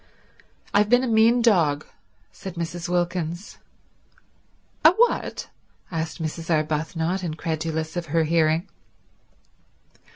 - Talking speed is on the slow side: Yes, slow, 100 wpm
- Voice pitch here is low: No, medium, 170 Hz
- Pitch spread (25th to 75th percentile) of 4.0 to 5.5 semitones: No, average, 3.1 semitones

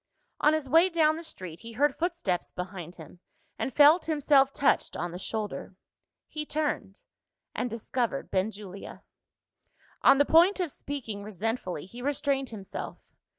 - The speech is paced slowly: No, average, 145 wpm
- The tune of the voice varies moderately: No, wide, 7.5 semitones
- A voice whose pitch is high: Yes, very high, 250 Hz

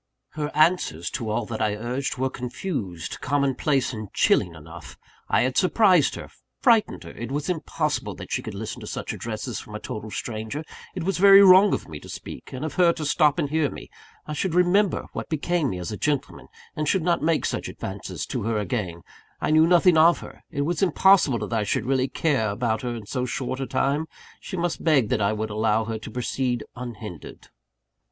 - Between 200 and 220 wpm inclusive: Yes, fast, 205 wpm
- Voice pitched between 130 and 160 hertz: Yes, low, 135 Hz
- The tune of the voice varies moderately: No, wide, 6.8 semitones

